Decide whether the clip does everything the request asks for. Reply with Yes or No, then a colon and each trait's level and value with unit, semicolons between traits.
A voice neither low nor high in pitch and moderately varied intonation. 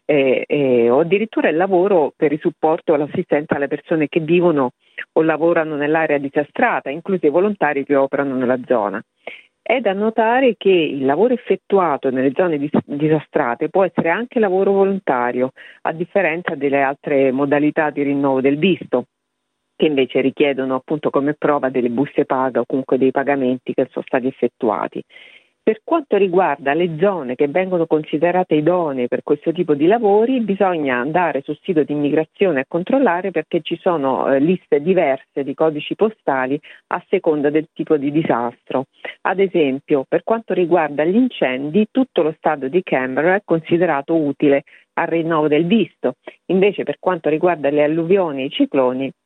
Yes: medium, 155 Hz; average, 4.6 semitones